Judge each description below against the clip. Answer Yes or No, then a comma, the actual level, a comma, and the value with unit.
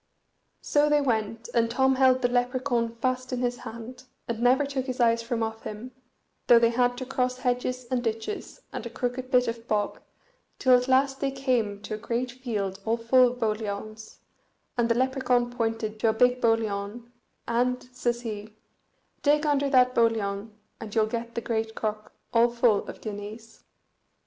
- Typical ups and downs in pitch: No, narrow, 2.2 semitones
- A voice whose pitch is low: No, high, 240 Hz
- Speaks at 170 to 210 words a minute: Yes, average, 180 wpm